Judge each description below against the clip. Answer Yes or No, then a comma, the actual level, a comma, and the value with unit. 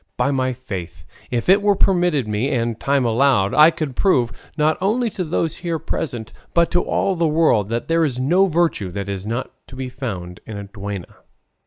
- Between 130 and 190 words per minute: No, average, 200 wpm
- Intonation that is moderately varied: No, wide, 7.3 semitones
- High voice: No, low, 130 Hz